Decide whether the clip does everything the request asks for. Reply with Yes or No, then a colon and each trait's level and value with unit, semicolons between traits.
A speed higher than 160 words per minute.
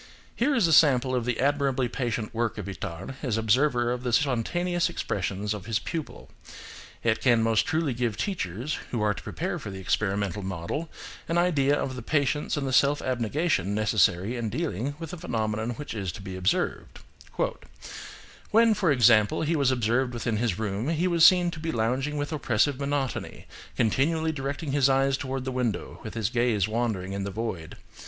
Yes: average, 185 wpm